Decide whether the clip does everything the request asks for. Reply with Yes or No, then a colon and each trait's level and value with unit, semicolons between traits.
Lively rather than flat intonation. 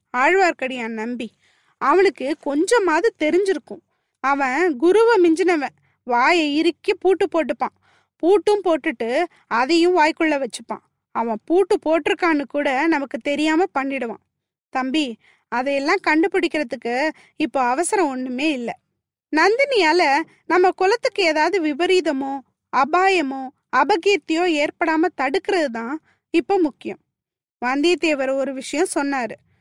No: average, 4.9 semitones